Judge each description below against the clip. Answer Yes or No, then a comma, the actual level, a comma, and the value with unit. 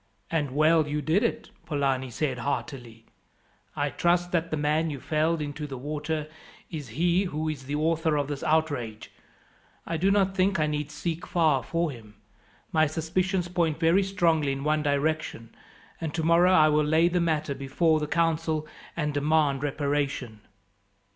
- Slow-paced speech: No, average, 165 wpm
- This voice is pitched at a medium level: Yes, medium, 155 Hz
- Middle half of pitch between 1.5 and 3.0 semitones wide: Yes, narrow, 2.5 semitones